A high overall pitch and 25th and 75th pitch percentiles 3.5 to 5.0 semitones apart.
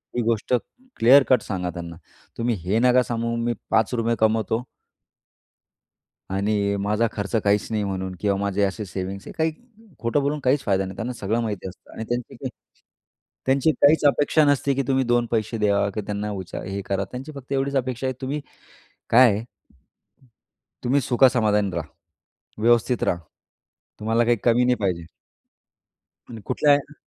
No: low, 115 Hz; average, 4.0 semitones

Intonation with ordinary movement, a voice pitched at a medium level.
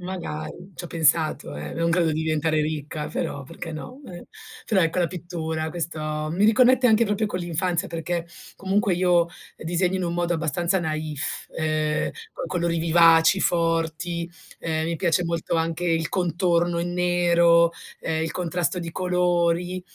No: narrow, 1.8 semitones; medium, 170 Hz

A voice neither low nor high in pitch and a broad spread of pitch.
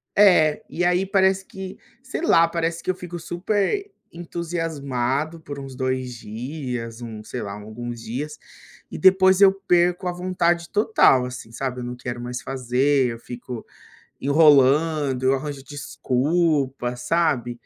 Yes: medium, 145 Hz; wide, 5.7 semitones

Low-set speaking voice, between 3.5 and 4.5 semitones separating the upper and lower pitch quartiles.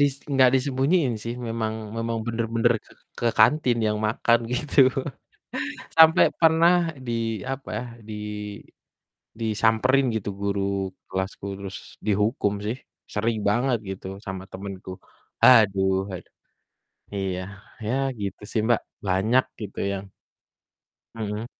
Yes: low, 110 Hz; average, 3.8 semitones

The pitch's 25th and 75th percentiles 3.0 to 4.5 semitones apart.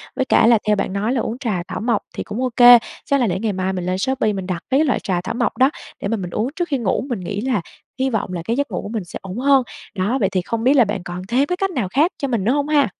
No: wide, 5.4 semitones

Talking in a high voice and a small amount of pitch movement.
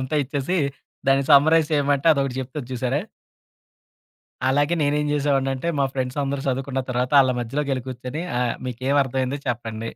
No: low, 135 Hz; narrow, 2.1 semitones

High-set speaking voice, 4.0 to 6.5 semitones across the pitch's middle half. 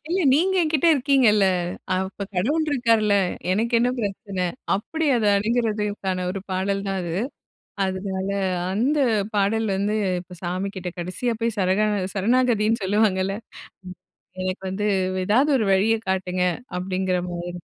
No: high, 200 Hz; average, 3.5 semitones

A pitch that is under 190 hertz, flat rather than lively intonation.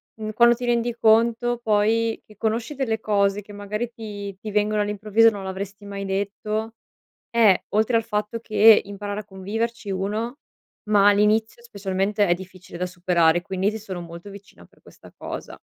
No: high, 210 Hz; narrow, 2.2 semitones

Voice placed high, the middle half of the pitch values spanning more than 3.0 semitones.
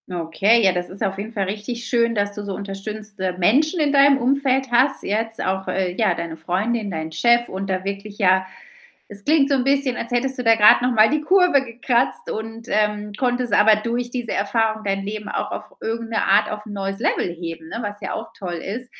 Yes: high, 215 Hz; average, 3.7 semitones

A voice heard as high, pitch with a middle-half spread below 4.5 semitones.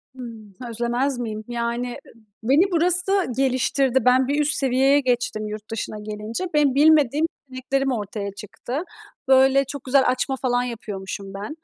Yes: very high, 255 Hz; average, 3.5 semitones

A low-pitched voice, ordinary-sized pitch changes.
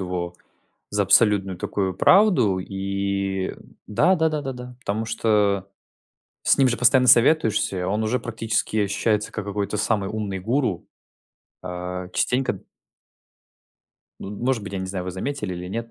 Yes: low, 105 Hz; average, 3.7 semitones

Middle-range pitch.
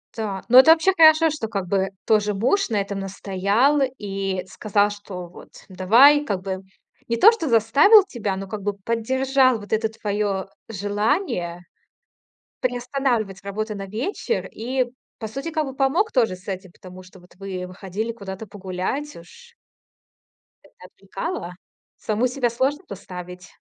No: high, 215 Hz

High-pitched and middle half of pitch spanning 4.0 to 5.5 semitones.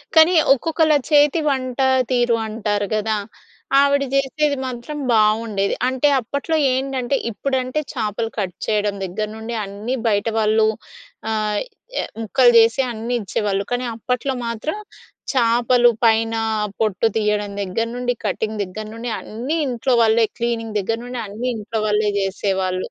No: high, 230 Hz; average, 3.3 semitones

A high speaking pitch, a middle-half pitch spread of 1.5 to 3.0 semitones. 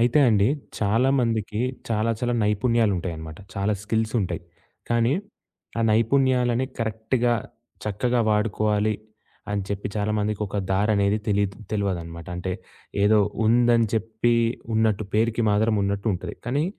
No: low, 110 Hz; narrow, 2.5 semitones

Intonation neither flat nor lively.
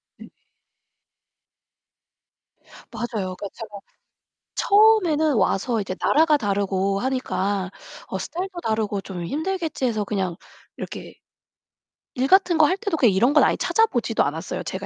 No: wide, 8.3 semitones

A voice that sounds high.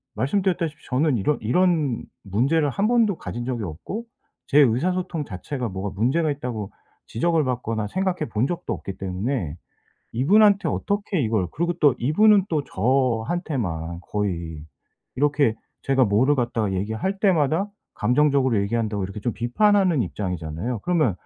No: low, 130 Hz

